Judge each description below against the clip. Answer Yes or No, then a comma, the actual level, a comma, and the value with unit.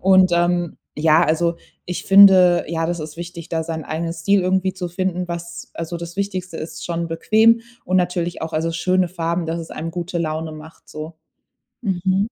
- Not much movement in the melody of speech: Yes, narrow, 2.0 semitones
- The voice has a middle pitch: Yes, medium, 170 Hz